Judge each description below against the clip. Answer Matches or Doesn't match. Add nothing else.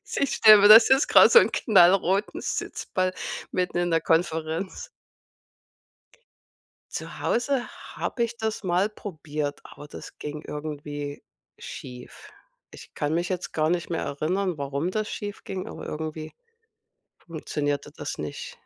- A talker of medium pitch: Matches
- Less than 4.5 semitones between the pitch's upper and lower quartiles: Doesn't match